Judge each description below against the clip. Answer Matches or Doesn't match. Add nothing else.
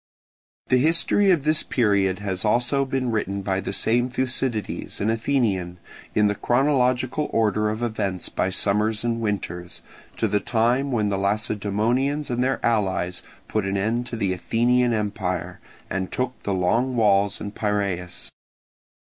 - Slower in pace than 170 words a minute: Matches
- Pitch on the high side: Doesn't match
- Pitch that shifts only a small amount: Doesn't match